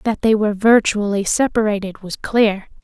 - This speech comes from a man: No, female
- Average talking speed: Yes, average, 150 wpm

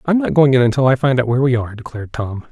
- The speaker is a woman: No, male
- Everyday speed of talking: No, fast, 310 wpm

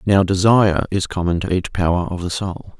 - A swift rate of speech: Yes, fast, 215 wpm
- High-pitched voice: No, very low, 95 Hz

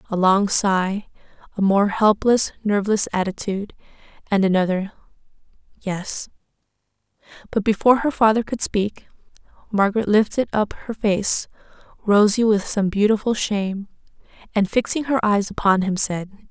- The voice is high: Yes, high, 205 Hz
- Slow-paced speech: Yes, slow, 125 wpm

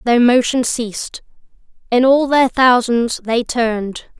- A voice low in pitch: No, high, 240 Hz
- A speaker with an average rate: No, slow, 130 wpm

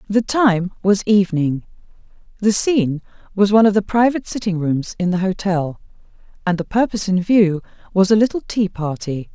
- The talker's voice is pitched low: No, high, 195 Hz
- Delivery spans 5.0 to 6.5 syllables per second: Yes, 5.4 syllables/s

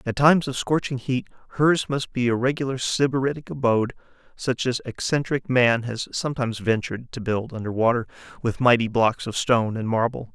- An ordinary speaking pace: Yes, average, 175 wpm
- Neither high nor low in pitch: No, low, 125 Hz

